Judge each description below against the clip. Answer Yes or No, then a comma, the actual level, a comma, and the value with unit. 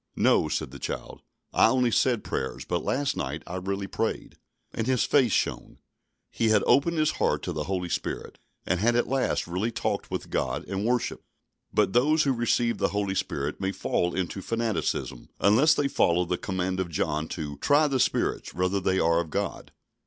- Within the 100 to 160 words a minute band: No, average, 190 wpm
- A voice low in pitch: Yes, low, 100 Hz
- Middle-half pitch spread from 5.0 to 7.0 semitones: Yes, wide, 5.4 semitones